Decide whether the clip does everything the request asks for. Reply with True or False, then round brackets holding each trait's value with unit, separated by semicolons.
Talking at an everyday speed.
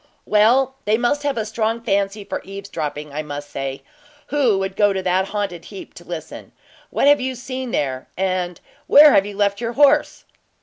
True (185 wpm)